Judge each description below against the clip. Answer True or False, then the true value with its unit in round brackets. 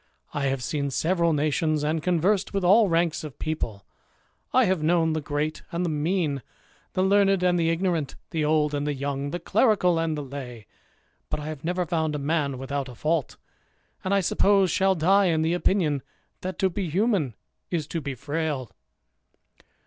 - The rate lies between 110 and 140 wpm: False (185 wpm)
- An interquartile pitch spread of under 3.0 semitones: False (3.8 semitones)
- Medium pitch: True (160 Hz)